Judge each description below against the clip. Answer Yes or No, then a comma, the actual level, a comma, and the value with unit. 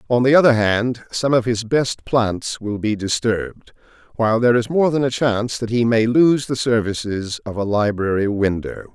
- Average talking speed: Yes, average, 195 wpm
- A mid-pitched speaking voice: No, low, 115 Hz